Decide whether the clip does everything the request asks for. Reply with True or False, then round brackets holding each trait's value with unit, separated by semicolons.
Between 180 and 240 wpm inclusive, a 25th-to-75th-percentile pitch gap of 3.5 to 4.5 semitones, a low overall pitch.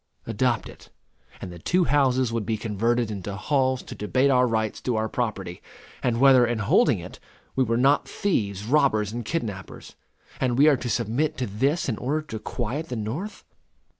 True (185 wpm; 4.0 semitones; 120 Hz)